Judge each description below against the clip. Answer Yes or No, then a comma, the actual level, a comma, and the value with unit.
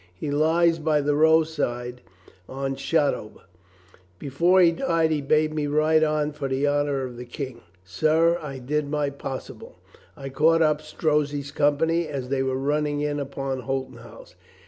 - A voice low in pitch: No, medium, 145 Hz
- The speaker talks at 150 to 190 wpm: Yes, average, 160 wpm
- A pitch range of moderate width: No, narrow, 2.3 semitones